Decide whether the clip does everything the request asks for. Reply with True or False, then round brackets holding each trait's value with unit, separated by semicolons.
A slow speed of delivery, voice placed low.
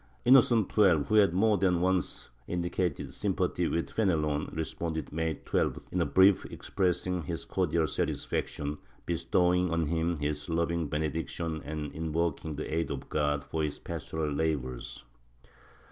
False (145 wpm; 80 Hz)